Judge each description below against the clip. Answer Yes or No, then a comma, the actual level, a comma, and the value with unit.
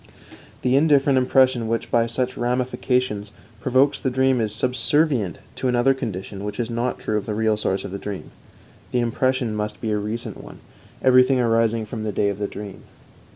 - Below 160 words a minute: No, average, 185 wpm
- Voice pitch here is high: No, low, 115 Hz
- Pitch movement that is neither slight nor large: Yes, average, 3.4 semitones